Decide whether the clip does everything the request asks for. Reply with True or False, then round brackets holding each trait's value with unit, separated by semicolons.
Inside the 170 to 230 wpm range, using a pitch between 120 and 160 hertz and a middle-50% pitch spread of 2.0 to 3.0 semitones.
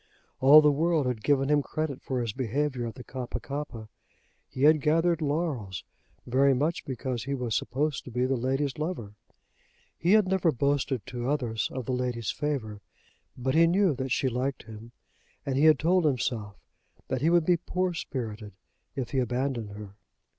False (180 wpm; 135 Hz; 3.8 semitones)